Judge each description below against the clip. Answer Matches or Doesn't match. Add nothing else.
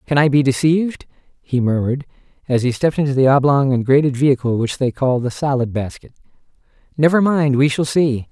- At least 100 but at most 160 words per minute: Doesn't match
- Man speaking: Matches